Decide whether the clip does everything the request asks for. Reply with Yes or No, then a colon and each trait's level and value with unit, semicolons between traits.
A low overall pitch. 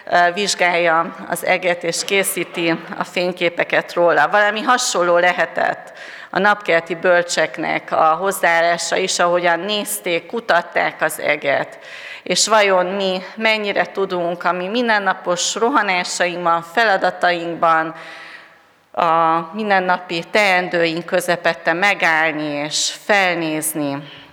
No: medium, 175 Hz